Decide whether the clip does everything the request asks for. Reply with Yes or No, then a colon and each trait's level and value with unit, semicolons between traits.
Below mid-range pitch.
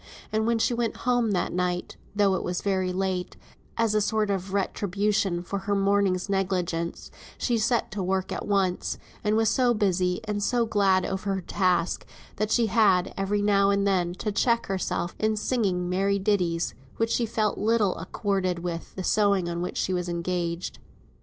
No: high, 195 Hz